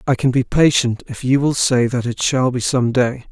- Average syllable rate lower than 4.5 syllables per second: No, 4.8 syllables/s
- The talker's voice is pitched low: Yes, low, 125 Hz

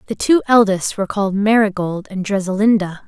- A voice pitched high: Yes, high, 200 Hz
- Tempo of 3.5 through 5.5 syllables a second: No, 5.7 syllables/s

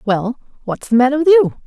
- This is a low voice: No, very high, 255 Hz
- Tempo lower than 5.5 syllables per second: No, 5.6 syllables/s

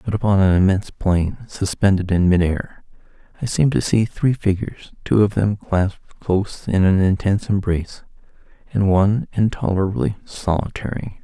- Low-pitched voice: Yes, low, 100 Hz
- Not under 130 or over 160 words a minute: Yes, average, 145 wpm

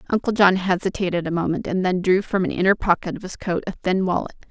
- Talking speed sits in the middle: No, fast, 240 wpm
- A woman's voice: Yes, female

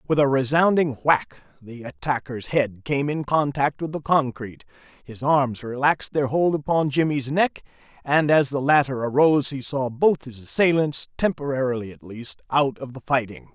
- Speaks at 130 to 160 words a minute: No, average, 170 wpm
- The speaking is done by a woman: No, male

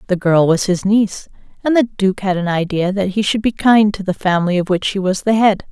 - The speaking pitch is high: Yes, high, 195 Hz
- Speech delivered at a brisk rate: Yes, fast, 265 wpm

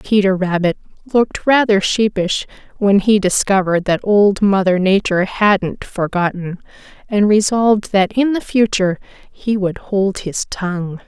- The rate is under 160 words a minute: Yes, average, 140 wpm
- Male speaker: No, female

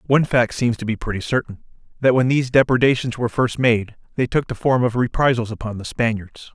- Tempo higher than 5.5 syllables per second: Yes, 6.0 syllables/s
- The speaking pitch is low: Yes, low, 120 Hz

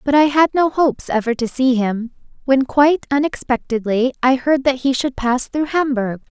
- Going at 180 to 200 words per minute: Yes, average, 190 wpm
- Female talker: Yes, female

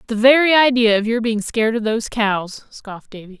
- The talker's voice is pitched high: Yes, high, 225 Hz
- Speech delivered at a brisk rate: Yes, fast, 210 wpm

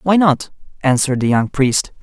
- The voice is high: No, medium, 145 Hz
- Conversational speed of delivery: Yes, average, 180 wpm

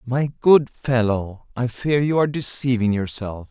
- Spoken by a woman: No, male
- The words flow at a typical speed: Yes, average, 155 wpm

